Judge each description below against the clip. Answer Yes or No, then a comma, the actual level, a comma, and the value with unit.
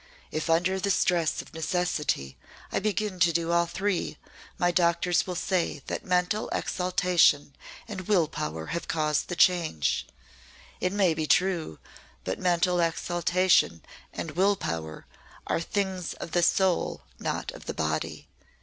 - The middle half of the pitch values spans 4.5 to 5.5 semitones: No, narrow, 2.4 semitones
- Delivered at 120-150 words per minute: Yes, average, 145 wpm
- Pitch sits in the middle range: Yes, medium, 175 Hz